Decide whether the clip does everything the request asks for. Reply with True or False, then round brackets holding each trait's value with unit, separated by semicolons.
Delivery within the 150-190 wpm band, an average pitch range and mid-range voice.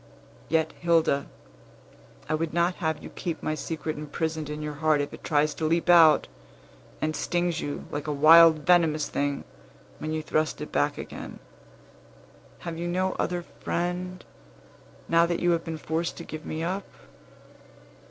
False (160 wpm; 1.9 semitones; 160 Hz)